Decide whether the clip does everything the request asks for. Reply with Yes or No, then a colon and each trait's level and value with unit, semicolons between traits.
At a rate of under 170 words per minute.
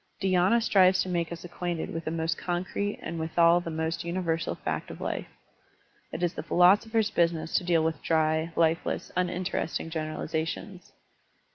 Yes: average, 155 wpm